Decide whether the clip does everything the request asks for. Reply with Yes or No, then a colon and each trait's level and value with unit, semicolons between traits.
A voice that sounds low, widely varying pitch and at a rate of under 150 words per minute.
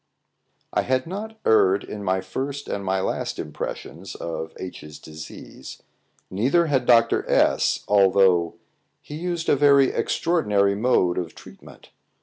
Yes: low, 105 Hz; wide, 7.2 semitones; slow, 135 wpm